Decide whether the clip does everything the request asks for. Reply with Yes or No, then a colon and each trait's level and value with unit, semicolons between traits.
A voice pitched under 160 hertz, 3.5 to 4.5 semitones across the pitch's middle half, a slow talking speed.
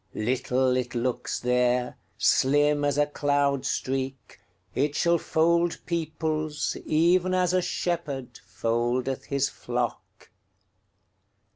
Yes: medium, 140 Hz; average, 4.0 semitones; slow, 85 wpm